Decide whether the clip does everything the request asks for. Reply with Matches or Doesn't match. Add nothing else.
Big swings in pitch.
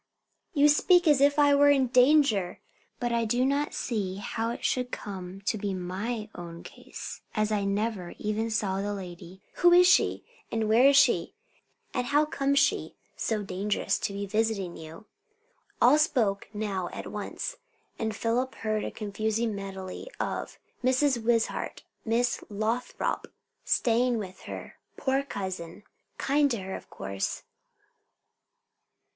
Doesn't match